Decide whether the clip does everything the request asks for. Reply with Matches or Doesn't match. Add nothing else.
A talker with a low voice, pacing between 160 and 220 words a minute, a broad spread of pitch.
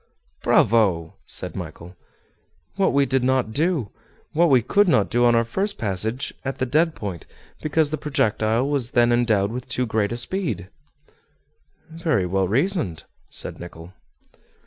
Doesn't match